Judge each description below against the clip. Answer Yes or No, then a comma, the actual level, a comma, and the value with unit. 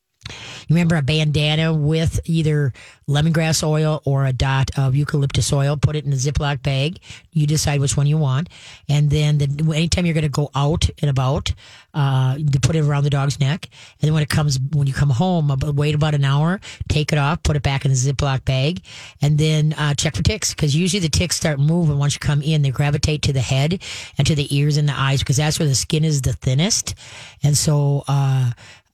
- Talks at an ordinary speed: No, fast, 220 wpm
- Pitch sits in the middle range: Yes, medium, 145 Hz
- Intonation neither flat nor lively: No, narrow, 2.0 semitones